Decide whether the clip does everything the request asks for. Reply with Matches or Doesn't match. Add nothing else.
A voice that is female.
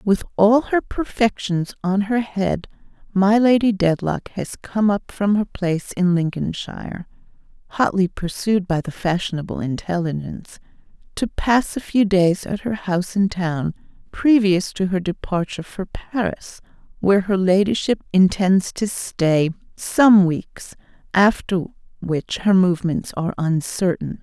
Matches